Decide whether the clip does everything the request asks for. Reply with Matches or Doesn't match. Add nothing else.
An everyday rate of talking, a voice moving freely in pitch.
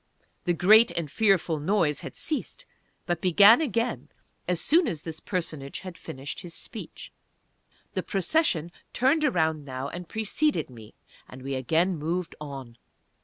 Matches